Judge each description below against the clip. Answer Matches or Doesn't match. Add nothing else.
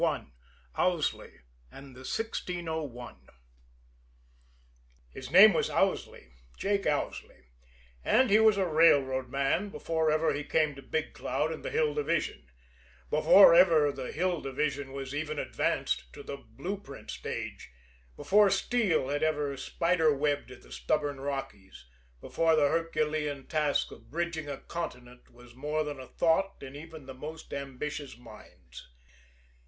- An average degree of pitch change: Matches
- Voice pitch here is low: Doesn't match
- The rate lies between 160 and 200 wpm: Doesn't match